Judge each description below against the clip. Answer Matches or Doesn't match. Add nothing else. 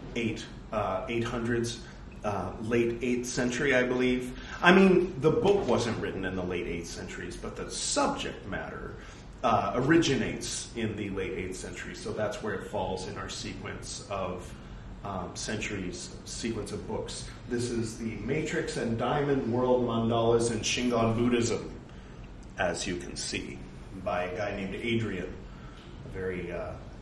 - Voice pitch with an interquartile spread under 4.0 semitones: Doesn't match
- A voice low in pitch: Matches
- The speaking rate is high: Doesn't match